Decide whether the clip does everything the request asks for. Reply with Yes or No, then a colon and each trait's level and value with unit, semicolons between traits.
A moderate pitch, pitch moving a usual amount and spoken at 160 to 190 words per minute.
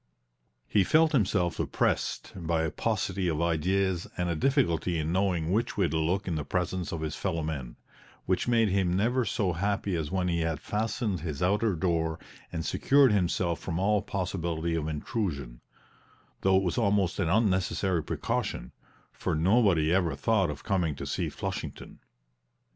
No: very low, 90 Hz; average, 3.6 semitones; average, 165 wpm